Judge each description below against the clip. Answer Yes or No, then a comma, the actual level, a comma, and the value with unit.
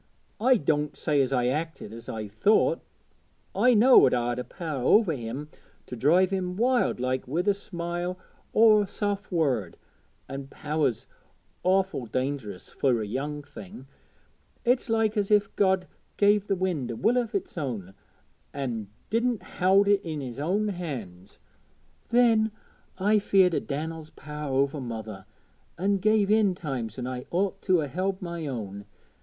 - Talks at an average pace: Yes, average, 160 wpm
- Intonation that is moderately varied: No, wide, 7.6 semitones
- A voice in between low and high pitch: Yes, medium, 160 Hz